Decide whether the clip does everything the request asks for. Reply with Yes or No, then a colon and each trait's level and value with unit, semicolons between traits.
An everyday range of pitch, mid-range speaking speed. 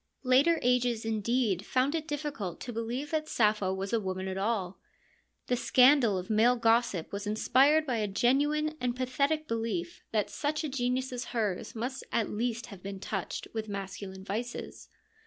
Yes: average, 4.3 semitones; average, 170 wpm